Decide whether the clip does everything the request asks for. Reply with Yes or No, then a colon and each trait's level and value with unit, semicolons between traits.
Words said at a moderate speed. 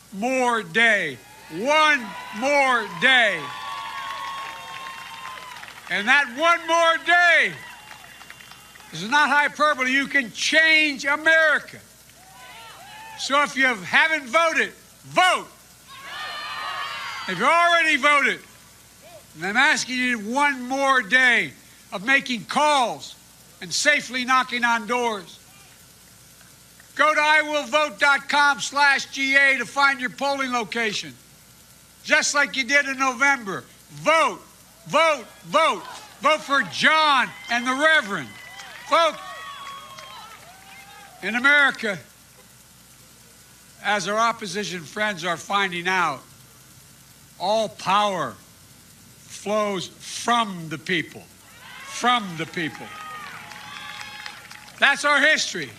No: slow, 95 wpm